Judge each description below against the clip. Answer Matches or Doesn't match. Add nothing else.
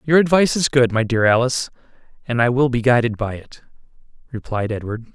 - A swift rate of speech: Doesn't match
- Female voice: Doesn't match